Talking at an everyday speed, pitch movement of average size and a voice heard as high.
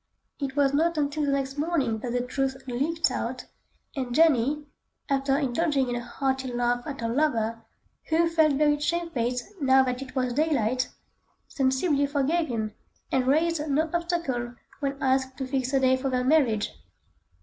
Yes: average, 165 wpm; average, 3.1 semitones; very high, 270 Hz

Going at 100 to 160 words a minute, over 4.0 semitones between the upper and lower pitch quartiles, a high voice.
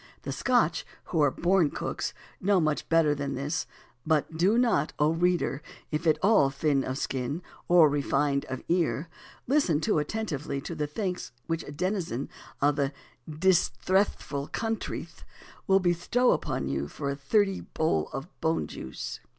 No: average, 155 wpm; average, 4.5 semitones; medium, 155 Hz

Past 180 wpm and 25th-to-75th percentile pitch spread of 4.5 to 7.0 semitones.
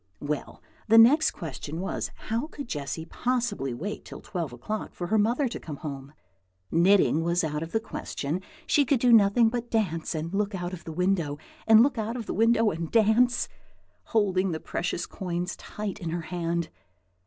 No: average, 175 wpm; wide, 5.5 semitones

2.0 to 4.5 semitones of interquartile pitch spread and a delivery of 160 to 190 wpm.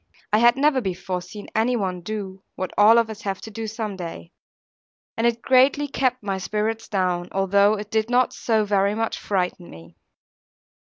Yes: average, 3.2 semitones; average, 180 wpm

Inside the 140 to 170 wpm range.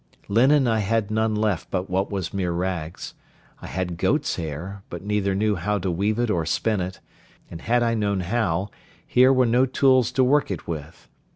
No: average, 195 wpm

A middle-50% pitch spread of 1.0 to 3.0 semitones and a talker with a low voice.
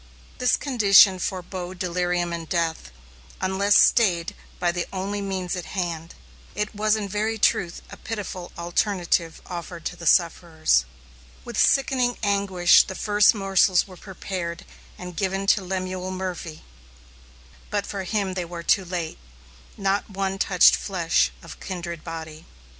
No: narrow, 2.4 semitones; medium, 185 Hz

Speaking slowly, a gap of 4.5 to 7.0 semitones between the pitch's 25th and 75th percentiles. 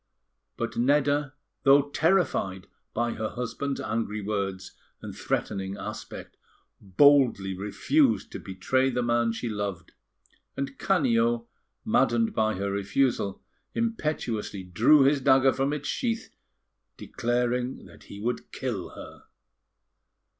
Yes: slow, 115 wpm; average, 5.2 semitones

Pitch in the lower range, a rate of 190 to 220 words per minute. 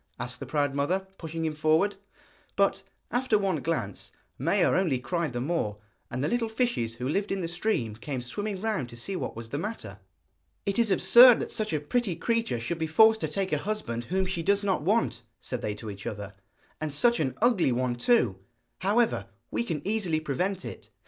No: medium, 170 Hz; average, 200 wpm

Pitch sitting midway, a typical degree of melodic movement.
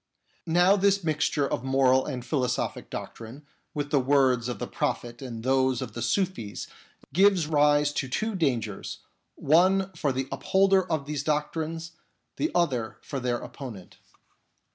Yes: medium, 145 Hz; average, 4.6 semitones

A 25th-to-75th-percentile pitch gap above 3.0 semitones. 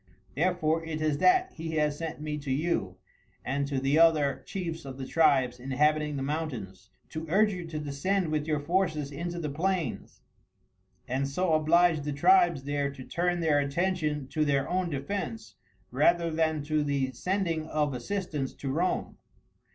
Yes: average, 3.4 semitones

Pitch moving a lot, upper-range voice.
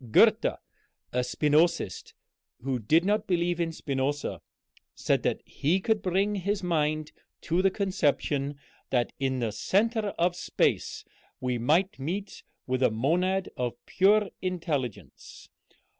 No: wide, 6.0 semitones; medium, 165 Hz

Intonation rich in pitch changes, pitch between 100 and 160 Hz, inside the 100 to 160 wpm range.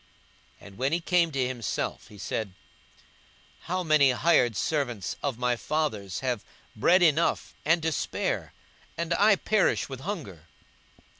Yes: wide, 6.3 semitones; medium, 140 Hz; average, 145 wpm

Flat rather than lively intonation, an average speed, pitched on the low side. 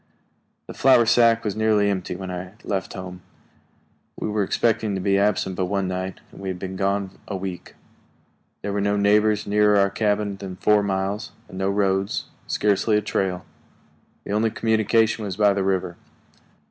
Yes: narrow, 1.8 semitones; average, 175 wpm; low, 100 Hz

